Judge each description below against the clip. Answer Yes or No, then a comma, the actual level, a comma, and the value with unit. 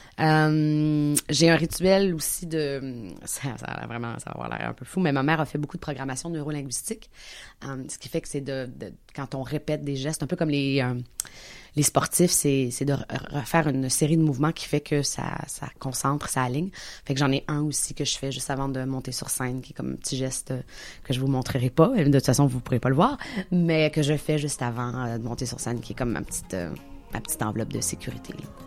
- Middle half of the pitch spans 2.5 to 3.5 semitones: Yes, average, 2.9 semitones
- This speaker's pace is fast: Yes, fast, 250 wpm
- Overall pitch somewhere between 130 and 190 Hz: Yes, medium, 140 Hz